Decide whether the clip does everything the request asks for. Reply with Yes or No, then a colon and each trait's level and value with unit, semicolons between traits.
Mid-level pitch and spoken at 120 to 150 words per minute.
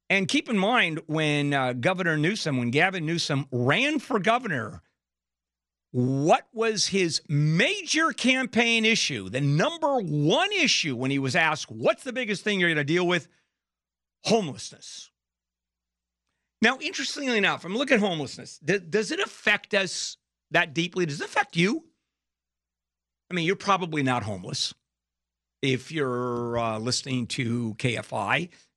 Yes: medium, 155 Hz; average, 140 wpm